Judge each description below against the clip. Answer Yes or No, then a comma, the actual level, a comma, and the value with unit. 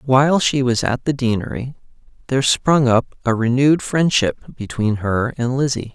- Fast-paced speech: No, average, 160 wpm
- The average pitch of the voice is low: Yes, low, 125 Hz